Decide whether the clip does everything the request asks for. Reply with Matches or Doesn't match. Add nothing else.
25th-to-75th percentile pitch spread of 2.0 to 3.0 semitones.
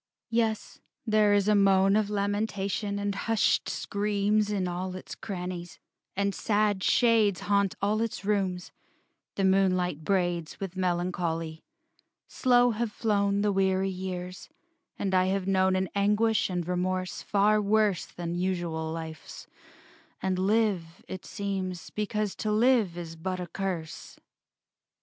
Matches